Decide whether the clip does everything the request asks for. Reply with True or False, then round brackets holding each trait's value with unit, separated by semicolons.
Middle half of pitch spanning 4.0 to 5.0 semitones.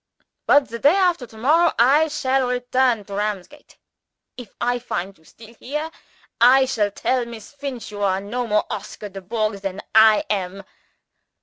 True (4.4 semitones)